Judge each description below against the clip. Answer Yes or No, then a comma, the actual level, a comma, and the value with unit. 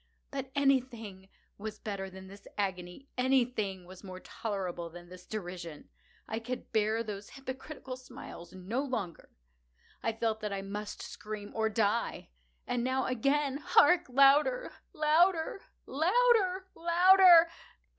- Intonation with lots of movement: Yes, wide, 6.1 semitones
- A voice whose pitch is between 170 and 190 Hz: No, high, 225 Hz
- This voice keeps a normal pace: No, slow, 120 wpm